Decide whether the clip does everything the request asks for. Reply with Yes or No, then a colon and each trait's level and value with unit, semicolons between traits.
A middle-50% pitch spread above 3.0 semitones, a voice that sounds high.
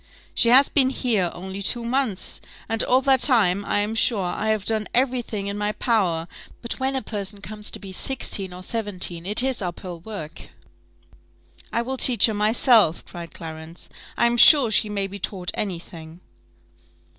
Yes: average, 4.4 semitones; high, 210 Hz